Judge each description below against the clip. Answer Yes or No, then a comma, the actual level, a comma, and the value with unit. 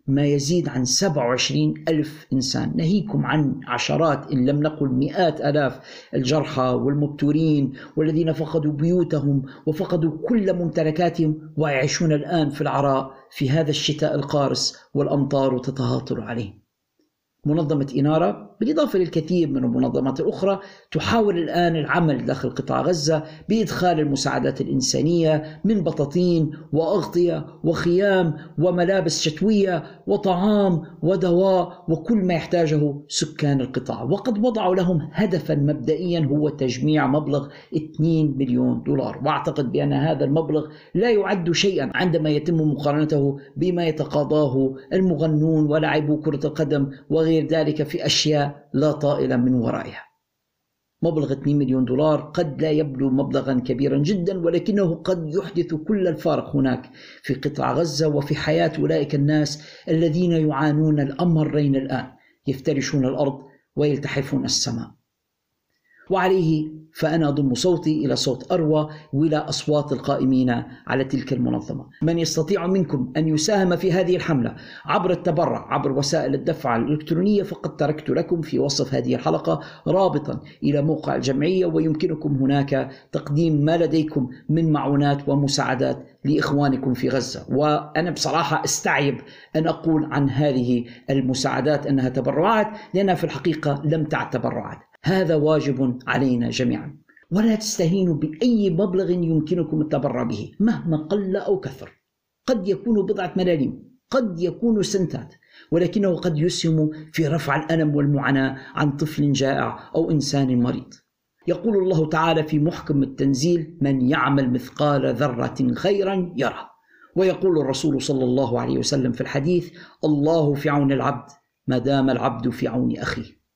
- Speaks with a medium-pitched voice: Yes, medium, 155 Hz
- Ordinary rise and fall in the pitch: Yes, average, 3.7 semitones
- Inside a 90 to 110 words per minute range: No, average, 125 wpm